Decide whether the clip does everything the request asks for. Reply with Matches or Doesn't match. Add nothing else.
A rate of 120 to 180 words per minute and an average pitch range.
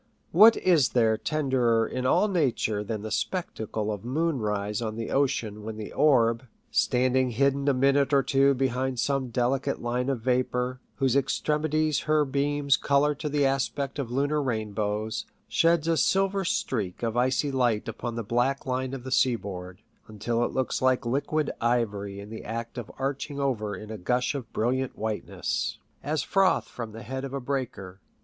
Matches